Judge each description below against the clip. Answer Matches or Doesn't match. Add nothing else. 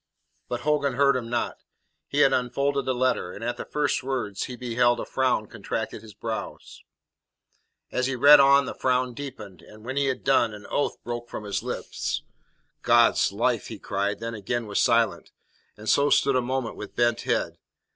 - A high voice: Doesn't match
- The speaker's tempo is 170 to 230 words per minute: Matches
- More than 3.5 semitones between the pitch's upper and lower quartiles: Doesn't match